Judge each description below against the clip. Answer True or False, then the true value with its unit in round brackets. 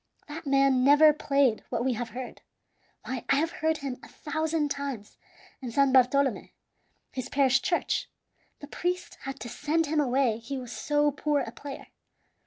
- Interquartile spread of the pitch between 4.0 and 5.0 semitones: False (2.6 semitones)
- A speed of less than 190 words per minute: True (170 wpm)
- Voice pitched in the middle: False (275 Hz)